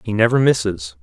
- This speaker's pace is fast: No, average, 175 wpm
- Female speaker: No, male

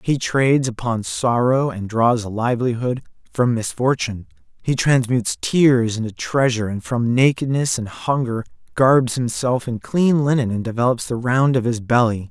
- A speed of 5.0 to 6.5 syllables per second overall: No, 4.8 syllables/s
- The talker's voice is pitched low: Yes, low, 120 Hz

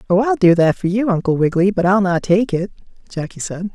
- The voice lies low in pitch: No, medium, 185 Hz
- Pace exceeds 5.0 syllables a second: Yes, 6.0 syllables/s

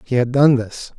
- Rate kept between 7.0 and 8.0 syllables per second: No, 4.7 syllables/s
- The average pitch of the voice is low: Yes, low, 125 Hz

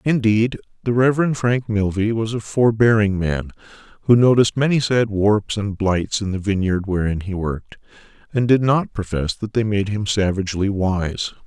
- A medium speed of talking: Yes, average, 165 wpm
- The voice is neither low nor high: No, low, 105 Hz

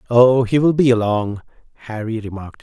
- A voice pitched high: No, low, 115 Hz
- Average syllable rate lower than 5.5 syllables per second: No, 5.6 syllables/s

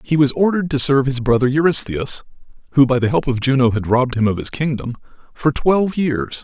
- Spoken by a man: Yes, male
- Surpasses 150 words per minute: Yes, average, 195 wpm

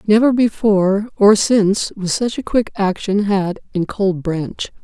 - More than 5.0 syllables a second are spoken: No, 4.0 syllables/s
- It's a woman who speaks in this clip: Yes, female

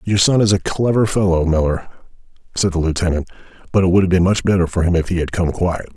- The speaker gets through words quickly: Yes, fast, 240 wpm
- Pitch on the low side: Yes, very low, 90 Hz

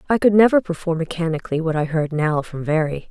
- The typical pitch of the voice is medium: Yes, medium, 165 Hz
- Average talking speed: No, fast, 215 wpm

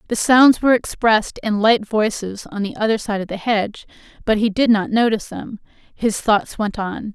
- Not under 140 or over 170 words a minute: No, average, 200 wpm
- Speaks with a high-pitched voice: Yes, high, 215 Hz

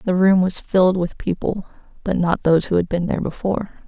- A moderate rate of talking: No, fast, 215 wpm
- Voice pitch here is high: No, medium, 180 Hz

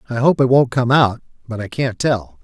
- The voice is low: Yes, low, 125 Hz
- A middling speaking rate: No, fast, 245 wpm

